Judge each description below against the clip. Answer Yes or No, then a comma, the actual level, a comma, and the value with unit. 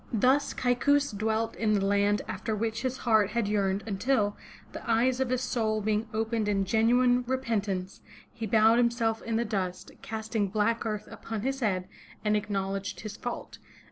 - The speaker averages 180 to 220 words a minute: No, average, 170 wpm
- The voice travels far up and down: No, narrow, 2.5 semitones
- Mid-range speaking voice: No, high, 220 Hz